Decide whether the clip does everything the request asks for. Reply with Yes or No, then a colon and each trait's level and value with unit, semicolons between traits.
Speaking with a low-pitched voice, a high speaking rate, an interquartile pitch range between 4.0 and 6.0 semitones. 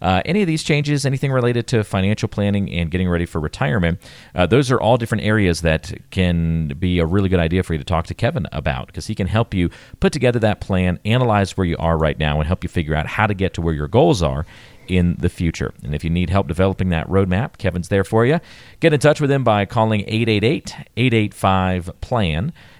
Yes: very low, 95 Hz; fast, 230 wpm; average, 4.7 semitones